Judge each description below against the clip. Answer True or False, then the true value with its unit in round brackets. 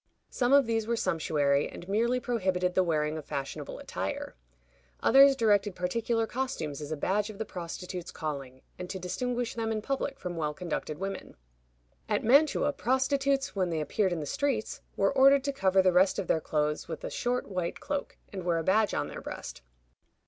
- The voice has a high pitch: True (195 Hz)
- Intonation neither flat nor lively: False (6.5 semitones)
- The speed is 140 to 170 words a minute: False (190 wpm)